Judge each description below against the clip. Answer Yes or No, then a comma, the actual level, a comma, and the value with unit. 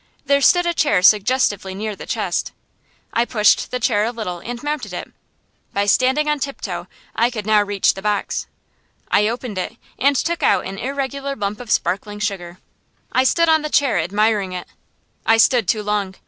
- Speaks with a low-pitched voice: No, high, 220 Hz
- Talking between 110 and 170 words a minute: No, average, 185 wpm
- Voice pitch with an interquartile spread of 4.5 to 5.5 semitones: Yes, average, 4.8 semitones